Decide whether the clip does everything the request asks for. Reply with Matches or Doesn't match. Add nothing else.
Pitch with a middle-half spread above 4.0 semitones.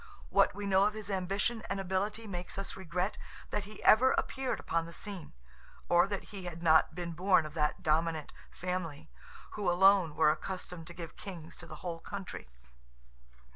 Doesn't match